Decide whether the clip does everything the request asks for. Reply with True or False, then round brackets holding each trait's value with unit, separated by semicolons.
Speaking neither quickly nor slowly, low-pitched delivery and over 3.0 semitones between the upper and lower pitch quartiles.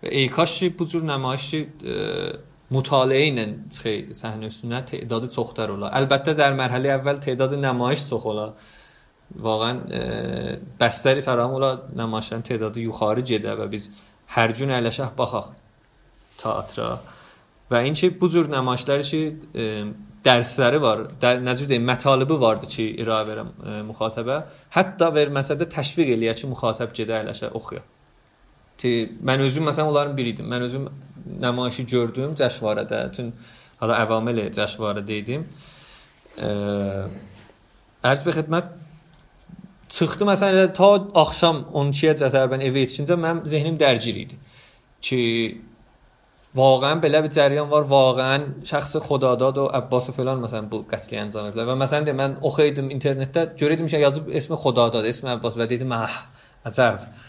True (130 wpm; 130 Hz; 4.4 semitones)